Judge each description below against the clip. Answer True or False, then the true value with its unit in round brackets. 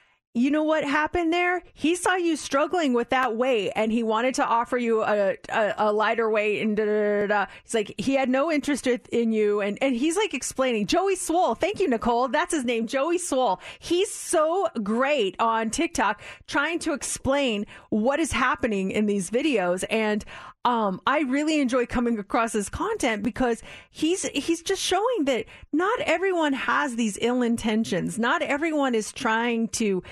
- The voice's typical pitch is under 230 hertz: False (255 Hz)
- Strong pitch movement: True (5.9 semitones)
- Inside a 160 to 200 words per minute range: True (180 wpm)